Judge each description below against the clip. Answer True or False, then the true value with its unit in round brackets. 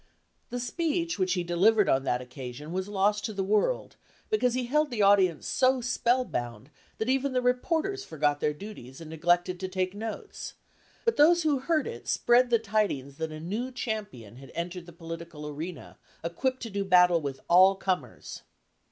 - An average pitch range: False (7.4 semitones)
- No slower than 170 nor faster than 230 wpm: True (180 wpm)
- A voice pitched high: True (195 Hz)